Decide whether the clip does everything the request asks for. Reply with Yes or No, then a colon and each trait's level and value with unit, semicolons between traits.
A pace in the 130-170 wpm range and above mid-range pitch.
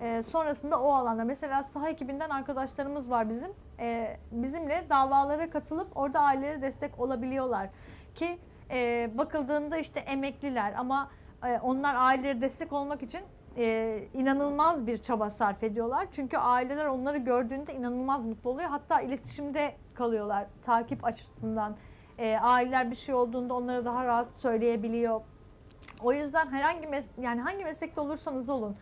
Yes: average, 135 wpm; very high, 270 Hz